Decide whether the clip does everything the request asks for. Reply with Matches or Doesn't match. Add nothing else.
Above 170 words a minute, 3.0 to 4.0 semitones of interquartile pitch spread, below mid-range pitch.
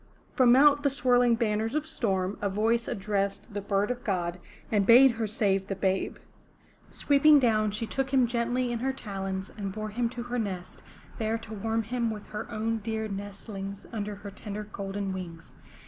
Doesn't match